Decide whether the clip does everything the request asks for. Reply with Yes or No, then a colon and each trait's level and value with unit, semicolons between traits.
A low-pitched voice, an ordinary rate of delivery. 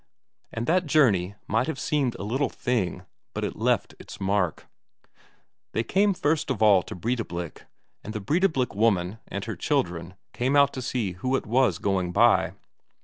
Yes: low, 115 Hz; average, 170 wpm